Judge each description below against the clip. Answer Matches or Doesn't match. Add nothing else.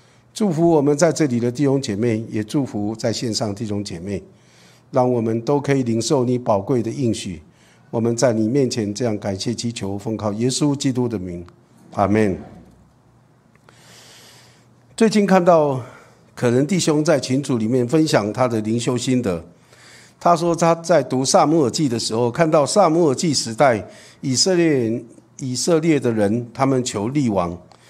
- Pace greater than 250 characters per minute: Doesn't match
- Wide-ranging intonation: Doesn't match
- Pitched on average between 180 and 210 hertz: Doesn't match